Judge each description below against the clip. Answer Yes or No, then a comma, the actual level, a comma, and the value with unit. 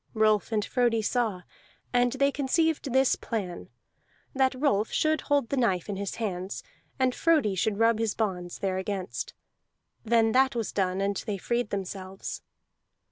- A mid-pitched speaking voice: No, high, 220 Hz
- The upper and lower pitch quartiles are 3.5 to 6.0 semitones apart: Yes, average, 4.7 semitones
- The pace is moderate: Yes, average, 150 wpm